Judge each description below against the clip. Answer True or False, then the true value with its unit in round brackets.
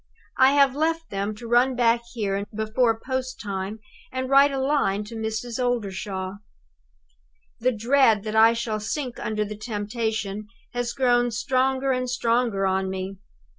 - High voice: True (230 Hz)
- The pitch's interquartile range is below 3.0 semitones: False (3.5 semitones)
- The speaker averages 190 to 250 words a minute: False (150 wpm)